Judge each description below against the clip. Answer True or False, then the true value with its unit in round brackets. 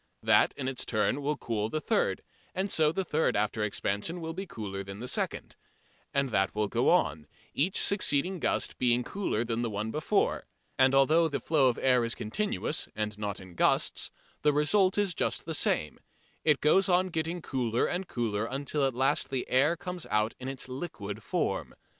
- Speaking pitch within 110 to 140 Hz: True (135 Hz)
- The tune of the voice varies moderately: False (6.8 semitones)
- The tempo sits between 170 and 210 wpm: True (190 wpm)